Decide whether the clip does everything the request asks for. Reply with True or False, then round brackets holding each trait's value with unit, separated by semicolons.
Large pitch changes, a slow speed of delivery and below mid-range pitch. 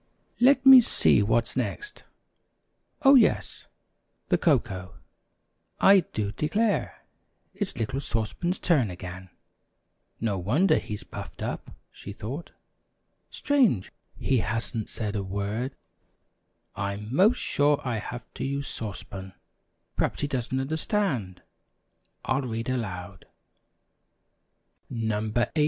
True (6.9 semitones; 115 wpm; 120 Hz)